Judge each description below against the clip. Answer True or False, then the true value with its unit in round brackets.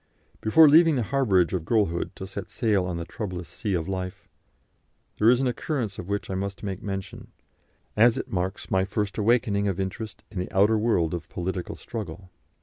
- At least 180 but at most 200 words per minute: True (190 wpm)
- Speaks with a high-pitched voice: False (100 Hz)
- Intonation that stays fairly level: False (3.2 semitones)